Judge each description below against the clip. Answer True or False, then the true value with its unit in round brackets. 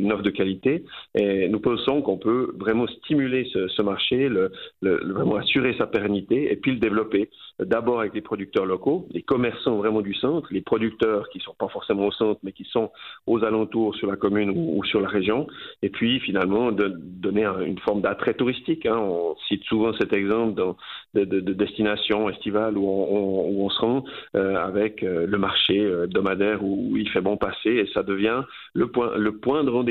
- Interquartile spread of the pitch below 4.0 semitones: True (2.6 semitones)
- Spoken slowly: False (200 wpm)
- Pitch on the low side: True (105 Hz)